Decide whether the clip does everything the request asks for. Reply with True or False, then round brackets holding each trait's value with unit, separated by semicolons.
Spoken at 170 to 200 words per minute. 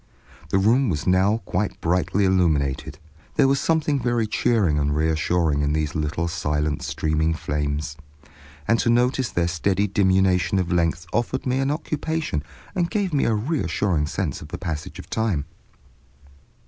False (155 wpm)